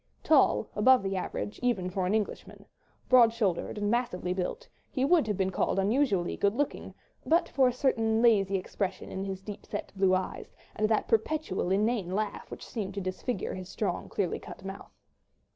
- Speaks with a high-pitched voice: Yes, high, 205 Hz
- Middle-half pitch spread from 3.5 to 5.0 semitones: Yes, average, 4.0 semitones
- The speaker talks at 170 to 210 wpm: Yes, average, 180 wpm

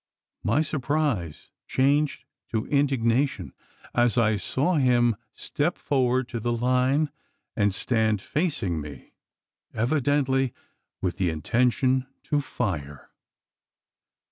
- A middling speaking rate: No, slow, 100 wpm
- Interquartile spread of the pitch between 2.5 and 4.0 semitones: No, average, 4.4 semitones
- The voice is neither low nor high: No, low, 125 Hz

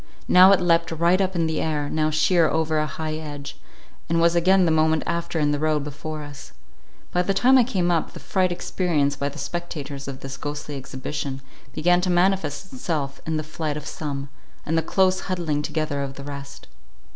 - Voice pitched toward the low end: No, medium, 155 Hz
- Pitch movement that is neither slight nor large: Yes, average, 3.2 semitones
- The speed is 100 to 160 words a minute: No, fast, 205 wpm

